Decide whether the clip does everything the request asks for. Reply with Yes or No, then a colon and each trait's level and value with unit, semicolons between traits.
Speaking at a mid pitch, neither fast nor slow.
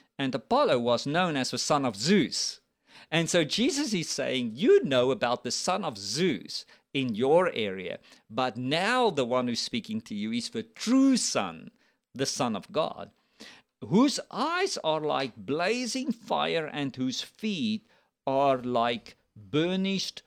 Yes: medium, 165 Hz; average, 155 wpm